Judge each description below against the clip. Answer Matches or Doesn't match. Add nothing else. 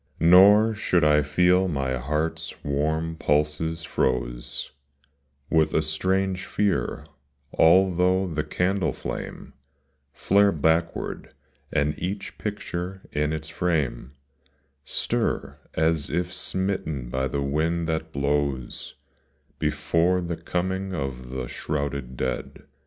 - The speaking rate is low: Matches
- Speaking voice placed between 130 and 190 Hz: Doesn't match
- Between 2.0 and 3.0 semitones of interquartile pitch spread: Doesn't match